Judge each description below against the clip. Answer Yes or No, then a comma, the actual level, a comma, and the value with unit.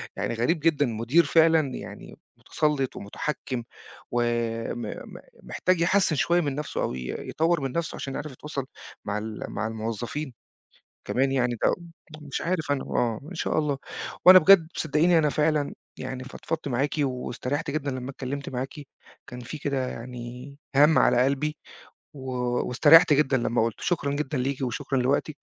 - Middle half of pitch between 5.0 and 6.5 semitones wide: No, average, 3.7 semitones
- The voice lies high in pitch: No, medium, 140 Hz